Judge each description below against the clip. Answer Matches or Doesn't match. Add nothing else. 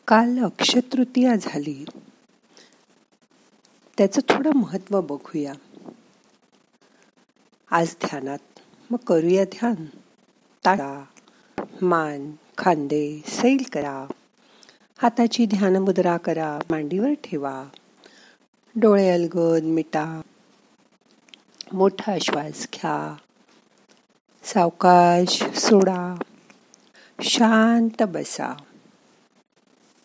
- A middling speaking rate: Doesn't match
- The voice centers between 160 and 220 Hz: Matches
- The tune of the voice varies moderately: Doesn't match